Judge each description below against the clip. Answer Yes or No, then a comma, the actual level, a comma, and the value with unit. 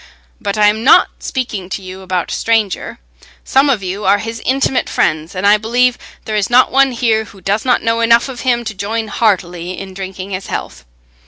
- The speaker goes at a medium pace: No, fast, 210 wpm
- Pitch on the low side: No, high, 215 Hz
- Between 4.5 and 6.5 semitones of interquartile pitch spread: No, average, 3.7 semitones